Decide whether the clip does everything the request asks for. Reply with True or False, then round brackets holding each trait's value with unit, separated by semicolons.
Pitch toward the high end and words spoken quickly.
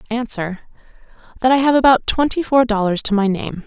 False (235 Hz; 165 wpm)